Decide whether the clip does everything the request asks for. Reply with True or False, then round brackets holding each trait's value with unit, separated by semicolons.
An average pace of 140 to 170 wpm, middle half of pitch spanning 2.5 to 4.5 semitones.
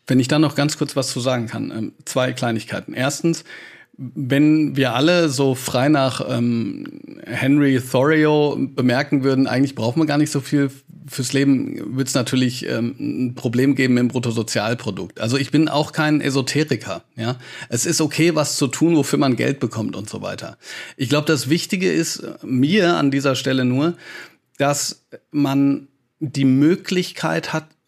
True (165 wpm; 2.9 semitones)